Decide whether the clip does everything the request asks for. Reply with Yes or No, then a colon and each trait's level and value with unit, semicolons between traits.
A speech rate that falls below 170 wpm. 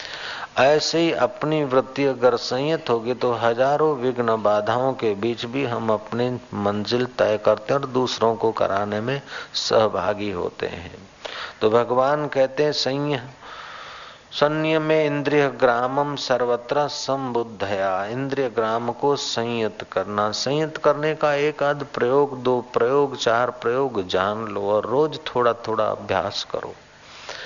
Yes: average, 130 wpm